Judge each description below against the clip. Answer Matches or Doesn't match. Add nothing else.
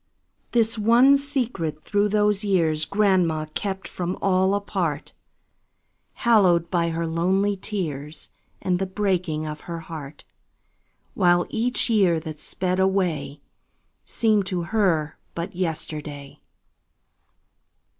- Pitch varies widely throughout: Doesn't match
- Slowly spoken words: Matches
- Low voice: Doesn't match